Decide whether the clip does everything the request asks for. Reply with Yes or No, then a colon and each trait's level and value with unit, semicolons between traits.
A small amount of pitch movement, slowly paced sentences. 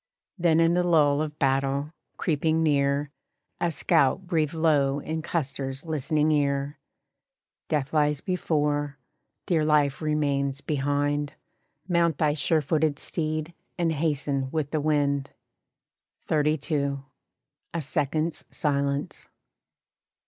Yes: narrow, 2.0 semitones; slow, 110 wpm